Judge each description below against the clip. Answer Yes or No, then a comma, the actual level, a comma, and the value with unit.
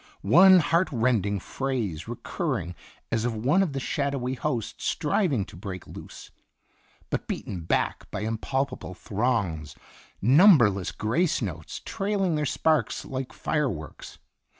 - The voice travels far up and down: Yes, wide, 6.8 semitones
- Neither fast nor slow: No, slow, 130 wpm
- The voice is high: No, low, 125 Hz